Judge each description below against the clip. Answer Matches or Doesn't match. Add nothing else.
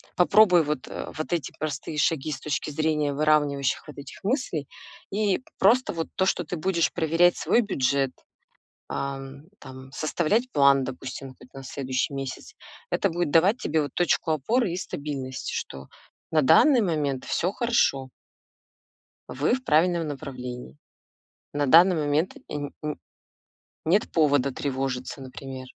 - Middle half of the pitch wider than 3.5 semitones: Matches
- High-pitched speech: Doesn't match